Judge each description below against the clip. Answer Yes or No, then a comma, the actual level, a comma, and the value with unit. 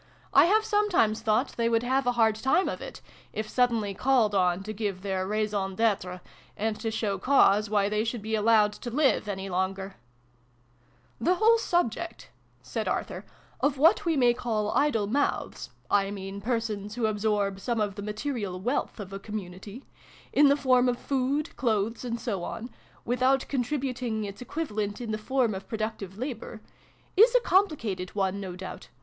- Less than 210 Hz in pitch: No, high, 220 Hz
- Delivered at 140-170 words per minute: No, average, 180 wpm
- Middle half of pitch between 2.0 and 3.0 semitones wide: No, average, 4.1 semitones